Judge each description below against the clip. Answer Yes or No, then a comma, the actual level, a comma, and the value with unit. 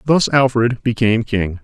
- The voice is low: Yes, low, 115 Hz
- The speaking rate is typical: Yes, average, 145 wpm